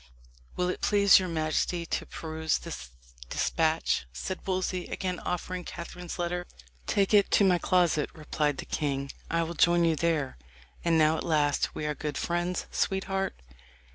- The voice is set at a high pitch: No, medium, 170 Hz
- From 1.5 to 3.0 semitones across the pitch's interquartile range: Yes, average, 2.7 semitones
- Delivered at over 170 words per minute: No, average, 160 wpm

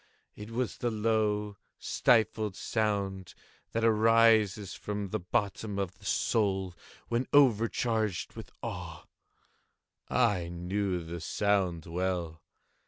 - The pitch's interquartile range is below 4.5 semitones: Yes, average, 3.1 semitones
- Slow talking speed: Yes, slow, 105 wpm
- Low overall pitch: Yes, low, 105 Hz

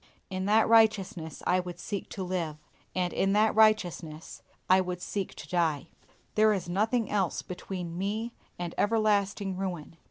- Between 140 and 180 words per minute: Yes, average, 155 wpm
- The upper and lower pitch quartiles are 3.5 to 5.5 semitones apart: No, average, 3.1 semitones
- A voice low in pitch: No, high, 190 Hz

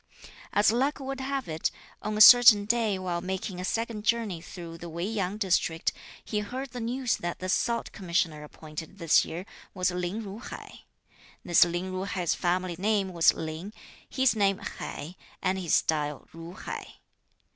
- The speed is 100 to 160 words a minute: No, average, 170 wpm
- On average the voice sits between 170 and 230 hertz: Yes, high, 190 Hz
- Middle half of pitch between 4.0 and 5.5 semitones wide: Yes, average, 4.4 semitones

